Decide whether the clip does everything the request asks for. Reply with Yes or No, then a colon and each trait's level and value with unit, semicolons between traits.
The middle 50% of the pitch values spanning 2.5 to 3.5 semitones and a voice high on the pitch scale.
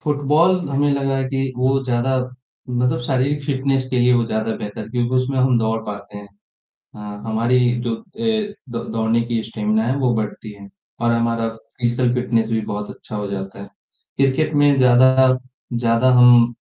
No: average, 2.9 semitones; low, 120 Hz